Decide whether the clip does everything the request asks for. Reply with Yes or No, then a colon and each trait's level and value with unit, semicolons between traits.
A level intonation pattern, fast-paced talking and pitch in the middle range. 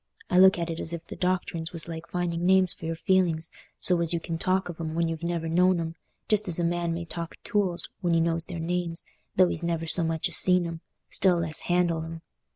Yes: narrow, 1.5 semitones; fast, 250 wpm; medium, 170 Hz